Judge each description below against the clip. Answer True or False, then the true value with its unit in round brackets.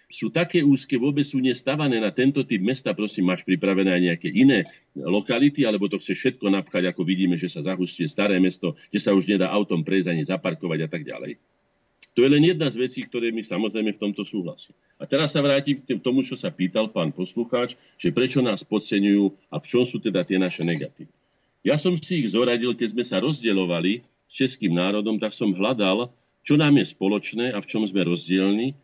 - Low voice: True (110 Hz)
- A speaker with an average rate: False (205 wpm)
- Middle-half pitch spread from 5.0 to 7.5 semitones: True (5.4 semitones)